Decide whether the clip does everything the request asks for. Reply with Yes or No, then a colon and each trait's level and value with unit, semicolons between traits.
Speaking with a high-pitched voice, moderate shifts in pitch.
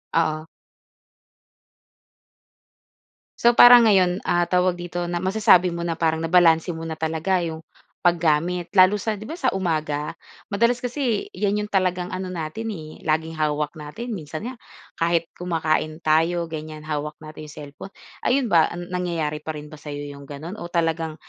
No: medium, 170 Hz; average, 3.0 semitones